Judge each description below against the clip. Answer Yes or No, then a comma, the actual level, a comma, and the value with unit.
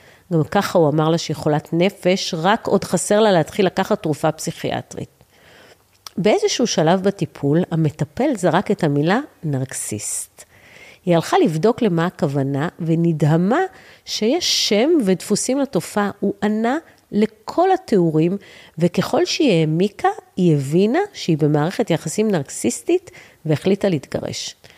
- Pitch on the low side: No, medium, 180 Hz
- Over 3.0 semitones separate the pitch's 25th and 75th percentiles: Yes, average, 4.6 semitones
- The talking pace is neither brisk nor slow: Yes, average, 120 wpm